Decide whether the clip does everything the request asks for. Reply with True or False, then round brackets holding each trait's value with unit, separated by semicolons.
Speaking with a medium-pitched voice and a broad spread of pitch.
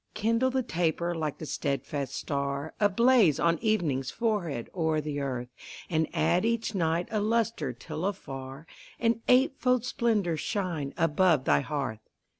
True (170 Hz; 7.4 semitones)